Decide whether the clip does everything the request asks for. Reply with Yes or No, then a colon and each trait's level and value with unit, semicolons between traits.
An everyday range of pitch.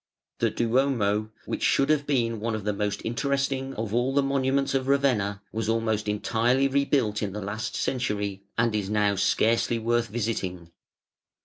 Yes: average, 4.2 semitones